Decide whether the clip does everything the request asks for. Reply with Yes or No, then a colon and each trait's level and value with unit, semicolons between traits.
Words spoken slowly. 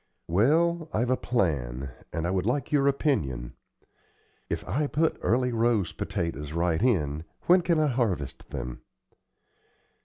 Yes: slow, 130 wpm